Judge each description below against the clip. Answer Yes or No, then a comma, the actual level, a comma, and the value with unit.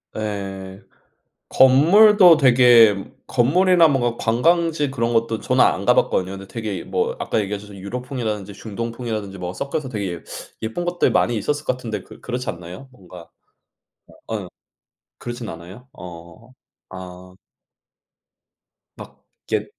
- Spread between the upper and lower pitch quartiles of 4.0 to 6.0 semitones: Yes, average, 5.1 semitones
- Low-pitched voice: Yes, low, 115 Hz